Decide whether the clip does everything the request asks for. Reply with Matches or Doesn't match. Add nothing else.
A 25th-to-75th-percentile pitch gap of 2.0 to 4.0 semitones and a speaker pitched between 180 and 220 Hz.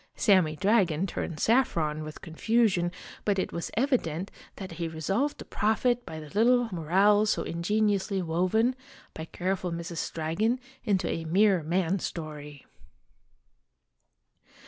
Doesn't match